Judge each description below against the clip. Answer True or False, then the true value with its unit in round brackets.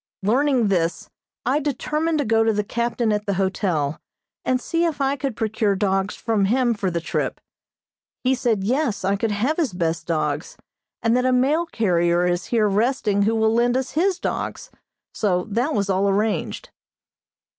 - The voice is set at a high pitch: True (220 Hz)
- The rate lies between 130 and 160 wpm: False (175 wpm)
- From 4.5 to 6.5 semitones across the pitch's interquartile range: True (4.9 semitones)